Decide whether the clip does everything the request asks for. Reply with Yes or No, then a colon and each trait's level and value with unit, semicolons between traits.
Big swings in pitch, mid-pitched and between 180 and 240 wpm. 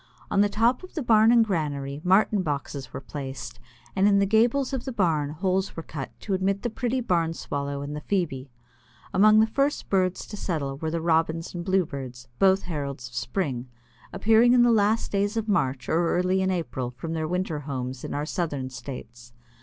Yes: wide, 6.4 semitones; medium, 175 Hz; average, 200 wpm